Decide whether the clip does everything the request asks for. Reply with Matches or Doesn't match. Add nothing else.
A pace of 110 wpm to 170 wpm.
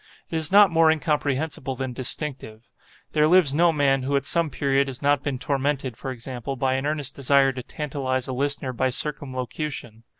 Doesn't match